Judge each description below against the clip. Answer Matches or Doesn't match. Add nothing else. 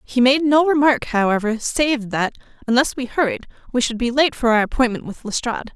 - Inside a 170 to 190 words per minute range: Doesn't match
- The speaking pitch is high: Matches